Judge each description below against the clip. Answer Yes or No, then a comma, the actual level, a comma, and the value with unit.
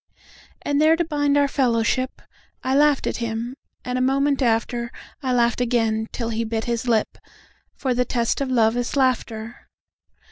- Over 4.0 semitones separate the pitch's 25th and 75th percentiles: No, average, 2.9 semitones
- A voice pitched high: Yes, high, 245 Hz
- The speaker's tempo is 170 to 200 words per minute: No, average, 150 wpm